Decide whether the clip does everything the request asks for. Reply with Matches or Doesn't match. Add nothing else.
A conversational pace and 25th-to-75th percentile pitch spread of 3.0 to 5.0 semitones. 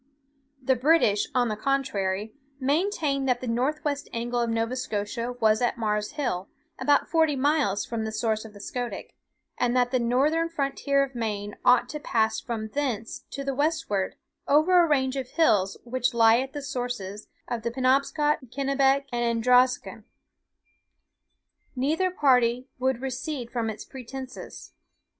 Matches